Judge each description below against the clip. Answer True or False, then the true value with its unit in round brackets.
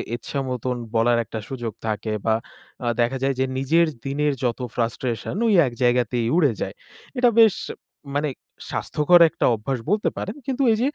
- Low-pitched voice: True (130 Hz)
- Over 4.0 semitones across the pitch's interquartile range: True (4.4 semitones)